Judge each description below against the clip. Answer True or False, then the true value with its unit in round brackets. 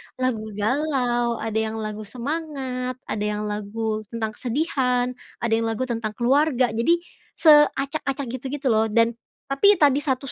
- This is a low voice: False (245 Hz)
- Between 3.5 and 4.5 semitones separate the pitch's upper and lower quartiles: True (3.9 semitones)